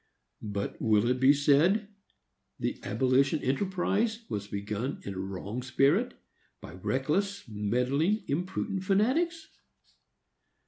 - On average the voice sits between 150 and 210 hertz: No, medium, 140 Hz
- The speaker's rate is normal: No, slow, 105 wpm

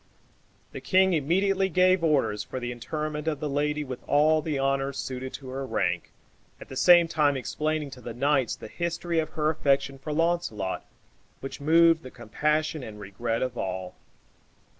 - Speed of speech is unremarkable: Yes, average, 170 wpm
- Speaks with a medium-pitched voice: Yes, medium, 145 Hz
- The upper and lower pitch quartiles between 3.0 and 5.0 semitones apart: Yes, average, 3.8 semitones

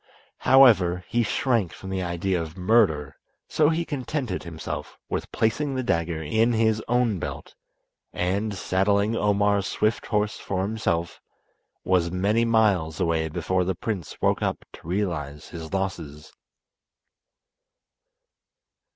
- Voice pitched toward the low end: Yes, very low, 95 Hz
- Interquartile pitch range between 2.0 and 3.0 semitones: No, average, 4.6 semitones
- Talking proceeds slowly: Yes, slow, 125 wpm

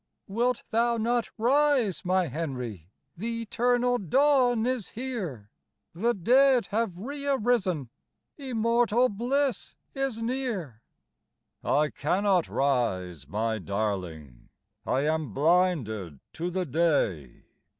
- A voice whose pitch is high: Yes, high, 195 Hz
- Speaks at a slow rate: Yes, slow, 105 wpm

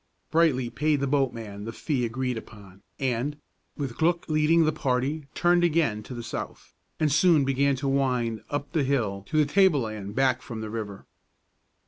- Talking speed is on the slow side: No, average, 170 wpm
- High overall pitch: No, low, 135 Hz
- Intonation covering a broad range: No, average, 4.8 semitones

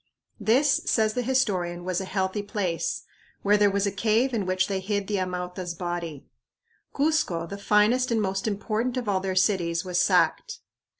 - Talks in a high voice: Yes, high, 200 Hz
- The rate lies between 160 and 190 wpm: Yes, average, 175 wpm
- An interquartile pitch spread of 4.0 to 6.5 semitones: No, average, 3.3 semitones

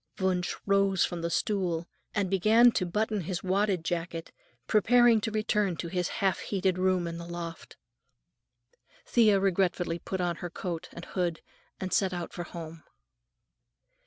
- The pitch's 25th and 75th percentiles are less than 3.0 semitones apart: Yes, narrow, 2.6 semitones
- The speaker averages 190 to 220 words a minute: No, average, 155 wpm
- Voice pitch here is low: No, medium, 185 Hz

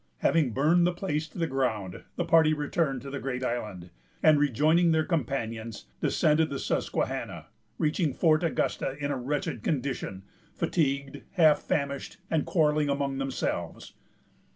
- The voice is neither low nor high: Yes, medium, 145 Hz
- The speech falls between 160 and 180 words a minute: No, average, 145 wpm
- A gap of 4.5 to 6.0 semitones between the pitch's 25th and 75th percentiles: No, average, 3.1 semitones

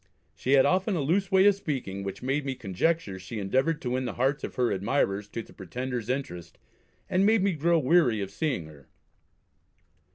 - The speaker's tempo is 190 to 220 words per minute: Yes, average, 195 wpm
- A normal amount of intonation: No, wide, 8.4 semitones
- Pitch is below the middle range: Yes, low, 130 Hz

